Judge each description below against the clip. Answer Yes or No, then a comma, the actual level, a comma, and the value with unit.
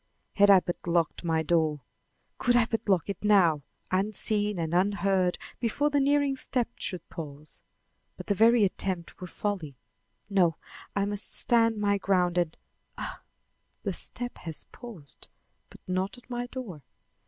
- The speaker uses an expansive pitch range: No, average, 4.6 semitones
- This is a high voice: Yes, high, 195 Hz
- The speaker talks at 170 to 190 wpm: No, average, 155 wpm